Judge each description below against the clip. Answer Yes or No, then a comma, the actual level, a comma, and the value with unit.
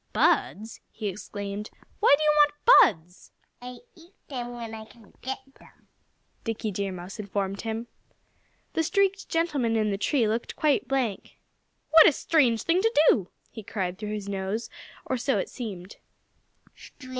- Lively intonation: Yes, wide, 5.8 semitones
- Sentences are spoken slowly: No, average, 155 wpm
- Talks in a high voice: Yes, high, 225 Hz